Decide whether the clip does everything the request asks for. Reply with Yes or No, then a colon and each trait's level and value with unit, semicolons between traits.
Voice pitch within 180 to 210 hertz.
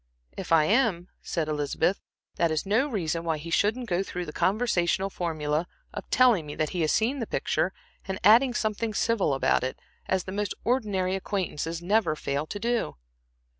Yes: medium, 185 Hz